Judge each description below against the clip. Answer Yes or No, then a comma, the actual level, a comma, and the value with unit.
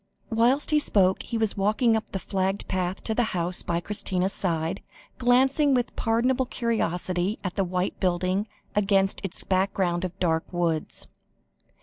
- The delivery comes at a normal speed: Yes, average, 150 wpm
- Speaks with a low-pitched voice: No, high, 195 Hz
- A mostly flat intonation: No, average, 3.8 semitones